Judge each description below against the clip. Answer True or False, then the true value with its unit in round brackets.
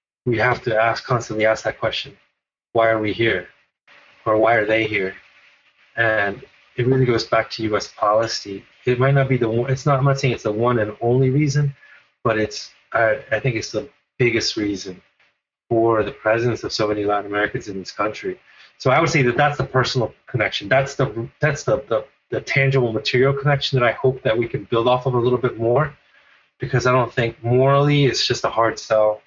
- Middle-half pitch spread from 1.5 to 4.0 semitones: True (3.3 semitones)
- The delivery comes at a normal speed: False (210 wpm)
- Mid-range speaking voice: False (120 Hz)